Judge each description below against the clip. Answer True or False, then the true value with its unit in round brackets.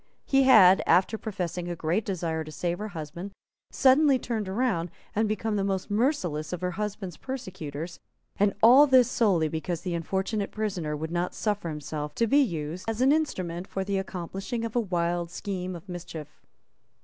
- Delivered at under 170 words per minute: False (175 wpm)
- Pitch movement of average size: True (4.3 semitones)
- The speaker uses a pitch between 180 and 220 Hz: True (190 Hz)